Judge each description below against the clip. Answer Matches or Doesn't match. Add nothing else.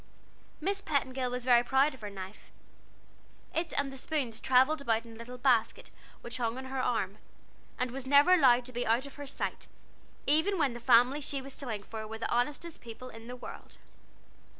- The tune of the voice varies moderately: Matches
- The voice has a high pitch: Matches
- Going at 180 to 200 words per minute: Matches